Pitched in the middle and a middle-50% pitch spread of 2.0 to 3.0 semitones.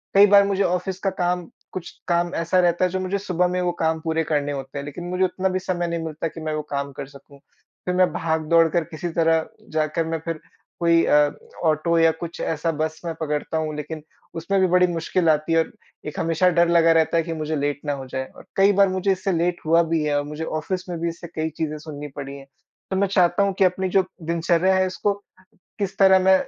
Yes: medium, 165 Hz; average, 2.7 semitones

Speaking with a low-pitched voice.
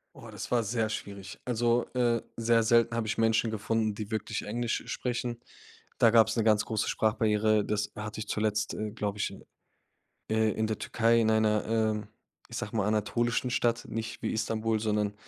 Yes: low, 110 Hz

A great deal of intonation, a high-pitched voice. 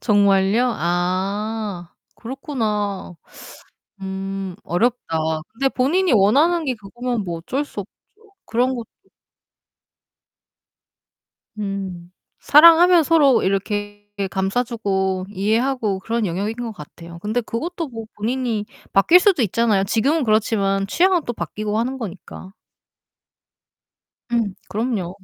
No: average, 4.5 semitones; high, 215 Hz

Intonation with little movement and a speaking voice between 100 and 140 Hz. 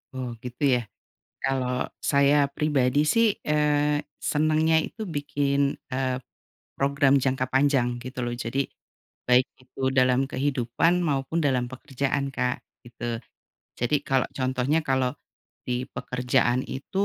Yes: narrow, 2.3 semitones; low, 135 Hz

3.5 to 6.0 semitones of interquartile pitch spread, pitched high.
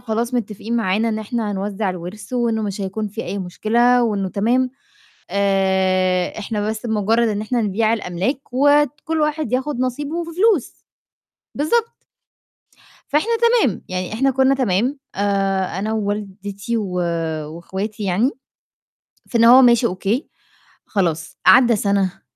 Yes: average, 4.2 semitones; high, 215 Hz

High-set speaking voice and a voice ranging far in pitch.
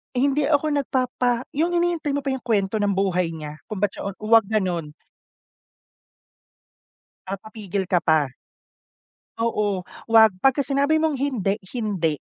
Yes: high, 220 Hz; wide, 6.2 semitones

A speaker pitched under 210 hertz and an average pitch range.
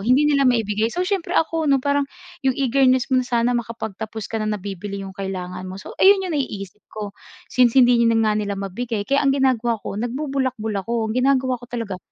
No: high, 235 Hz; average, 4.2 semitones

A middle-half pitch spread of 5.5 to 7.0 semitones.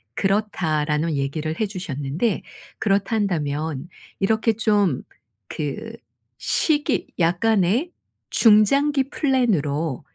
Yes: wide, 6.3 semitones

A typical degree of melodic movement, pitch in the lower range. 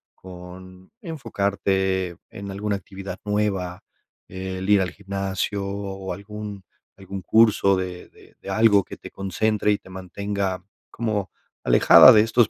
No: narrow, 1.7 semitones; low, 100 Hz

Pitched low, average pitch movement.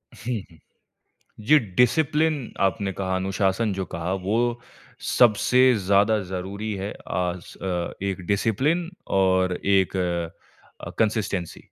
Yes: low, 100 Hz; average, 4.0 semitones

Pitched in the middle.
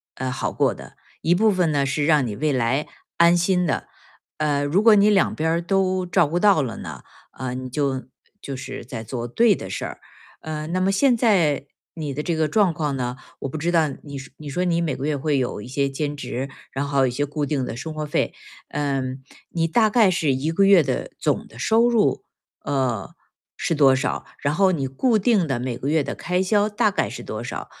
Yes: medium, 150 Hz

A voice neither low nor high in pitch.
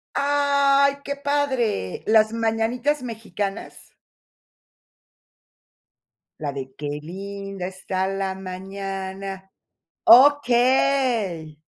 No: high, 210 Hz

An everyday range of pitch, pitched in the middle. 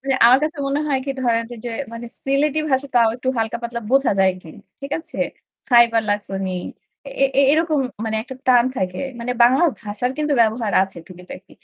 No: average, 3.8 semitones; high, 240 Hz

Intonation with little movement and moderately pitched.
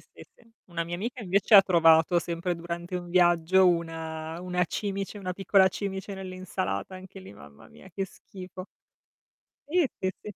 Yes: narrow, 2.2 semitones; medium, 180 Hz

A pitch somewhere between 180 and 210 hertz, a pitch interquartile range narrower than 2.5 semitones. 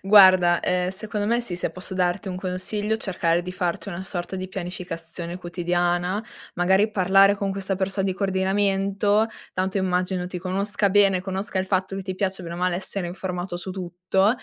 Yes: high, 190 Hz; narrow, 1.6 semitones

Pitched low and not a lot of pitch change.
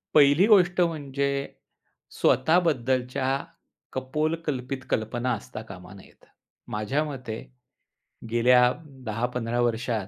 No: low, 130 Hz; average, 4.0 semitones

